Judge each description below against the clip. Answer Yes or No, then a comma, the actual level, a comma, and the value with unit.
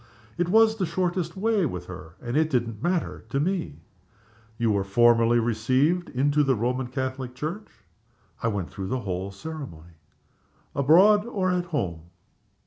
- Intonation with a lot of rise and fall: Yes, wide, 8.0 semitones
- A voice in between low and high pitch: No, low, 130 Hz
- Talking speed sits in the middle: Yes, average, 150 wpm